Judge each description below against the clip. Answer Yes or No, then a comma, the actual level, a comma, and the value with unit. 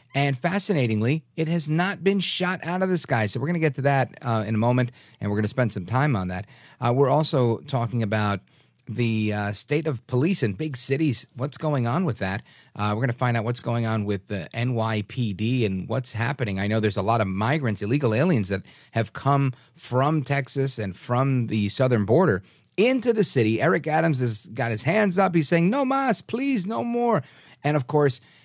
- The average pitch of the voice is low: Yes, low, 130 Hz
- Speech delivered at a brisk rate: Yes, fast, 215 wpm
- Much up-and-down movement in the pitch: Yes, wide, 5.8 semitones